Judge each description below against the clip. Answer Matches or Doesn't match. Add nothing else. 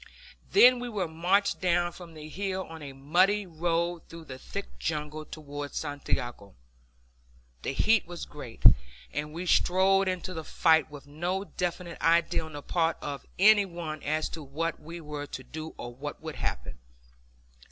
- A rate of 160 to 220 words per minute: Matches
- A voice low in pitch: Doesn't match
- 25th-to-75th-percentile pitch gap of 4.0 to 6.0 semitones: Doesn't match